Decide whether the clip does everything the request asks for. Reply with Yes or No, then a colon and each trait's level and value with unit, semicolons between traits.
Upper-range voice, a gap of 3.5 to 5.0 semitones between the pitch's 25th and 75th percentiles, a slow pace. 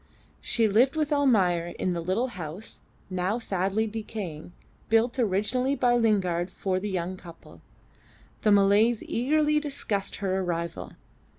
Yes: high, 205 Hz; average, 4.6 semitones; slow, 130 wpm